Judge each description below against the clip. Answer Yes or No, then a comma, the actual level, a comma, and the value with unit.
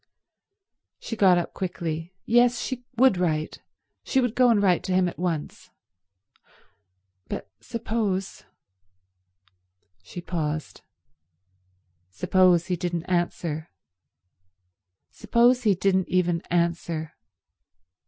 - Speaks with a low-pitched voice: No, medium, 180 Hz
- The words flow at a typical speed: No, slow, 100 wpm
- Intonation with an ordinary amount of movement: Yes, average, 3.9 semitones